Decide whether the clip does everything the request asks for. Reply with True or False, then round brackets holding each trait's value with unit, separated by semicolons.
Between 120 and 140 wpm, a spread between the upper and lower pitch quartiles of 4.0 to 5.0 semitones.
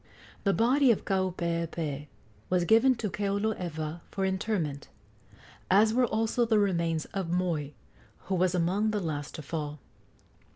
True (135 wpm; 4.5 semitones)